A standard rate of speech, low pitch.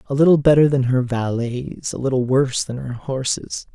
Yes: average, 190 wpm; low, 130 Hz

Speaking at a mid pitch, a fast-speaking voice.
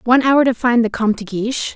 No: high, 235 Hz; fast, 275 wpm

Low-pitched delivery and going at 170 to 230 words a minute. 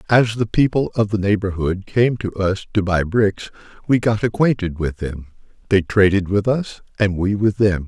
Yes: low, 100 Hz; average, 190 wpm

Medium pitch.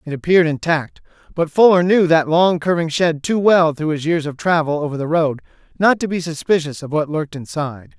Yes: medium, 160 Hz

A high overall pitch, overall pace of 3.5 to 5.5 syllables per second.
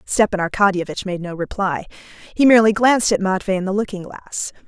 No: high, 200 Hz; 6.1 syllables/s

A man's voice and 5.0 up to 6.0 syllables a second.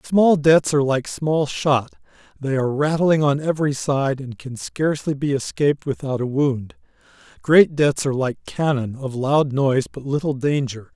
No: male; 4.8 syllables/s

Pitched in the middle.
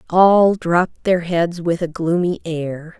Yes: medium, 170 Hz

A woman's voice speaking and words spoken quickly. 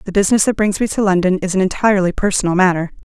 Yes: female; fast, 235 wpm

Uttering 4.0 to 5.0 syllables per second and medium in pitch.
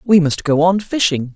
Yes: 4.8 syllables/s; medium, 165 Hz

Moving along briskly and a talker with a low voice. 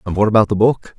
Yes: fast, 305 wpm; low, 105 Hz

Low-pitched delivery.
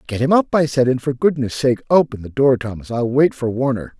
Yes: low, 130 Hz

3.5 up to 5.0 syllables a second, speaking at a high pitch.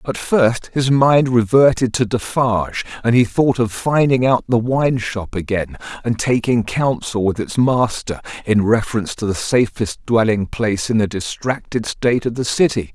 No: 4.6 syllables/s; low, 115 Hz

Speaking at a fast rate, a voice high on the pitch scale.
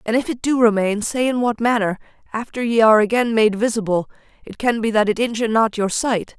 Yes: fast, 225 wpm; high, 225 Hz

